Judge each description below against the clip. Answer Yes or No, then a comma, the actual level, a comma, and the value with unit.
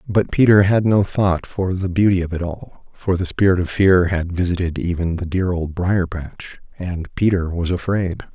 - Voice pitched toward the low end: Yes, very low, 90 Hz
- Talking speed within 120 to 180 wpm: No, average, 200 wpm